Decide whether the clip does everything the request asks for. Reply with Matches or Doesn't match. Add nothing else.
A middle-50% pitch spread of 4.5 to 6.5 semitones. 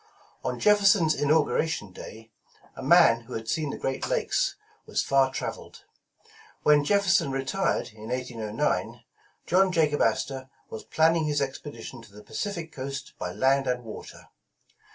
Matches